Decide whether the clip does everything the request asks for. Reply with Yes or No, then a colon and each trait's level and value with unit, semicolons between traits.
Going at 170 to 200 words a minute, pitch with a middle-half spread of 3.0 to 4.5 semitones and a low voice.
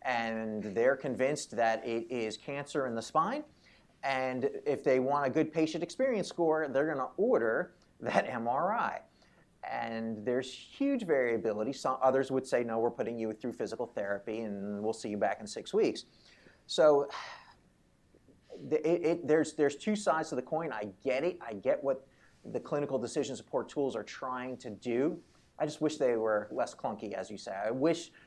No: average, 180 wpm; wide, 5.4 semitones; low, 130 Hz